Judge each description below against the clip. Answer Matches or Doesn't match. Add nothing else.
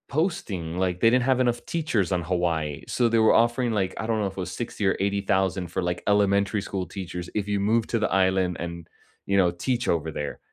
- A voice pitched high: Doesn't match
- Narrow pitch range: Doesn't match